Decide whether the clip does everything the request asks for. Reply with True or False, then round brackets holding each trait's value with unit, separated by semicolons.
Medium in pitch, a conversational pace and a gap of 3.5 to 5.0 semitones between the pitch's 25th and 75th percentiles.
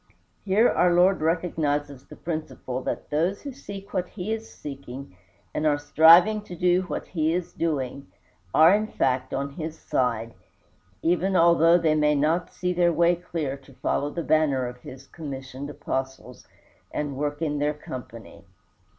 True (155 Hz; 160 wpm; 4.2 semitones)